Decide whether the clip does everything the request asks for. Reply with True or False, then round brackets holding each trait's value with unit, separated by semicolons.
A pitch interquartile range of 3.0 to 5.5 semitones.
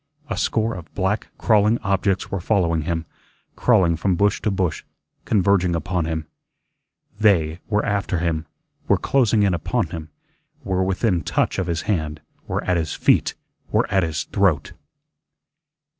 True (3.5 semitones)